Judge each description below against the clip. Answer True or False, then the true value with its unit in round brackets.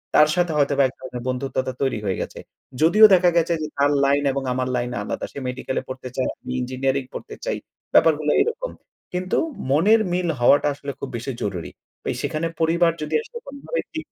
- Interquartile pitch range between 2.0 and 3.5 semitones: False (5.0 semitones)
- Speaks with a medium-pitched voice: True (145 Hz)